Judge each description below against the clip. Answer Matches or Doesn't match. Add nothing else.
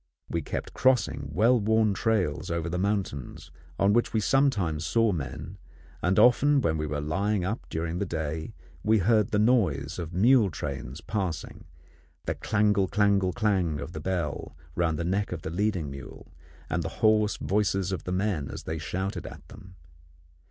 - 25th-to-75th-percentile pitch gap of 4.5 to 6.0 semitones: Matches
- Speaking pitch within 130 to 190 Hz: Doesn't match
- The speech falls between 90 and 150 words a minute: Doesn't match